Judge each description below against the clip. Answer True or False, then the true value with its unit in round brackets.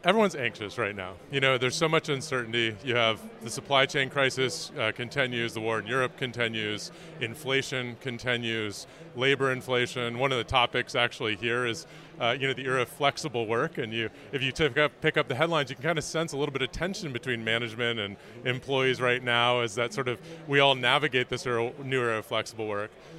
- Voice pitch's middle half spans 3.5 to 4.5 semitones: False (2.9 semitones)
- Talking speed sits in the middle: False (210 wpm)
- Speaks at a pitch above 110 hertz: True (130 Hz)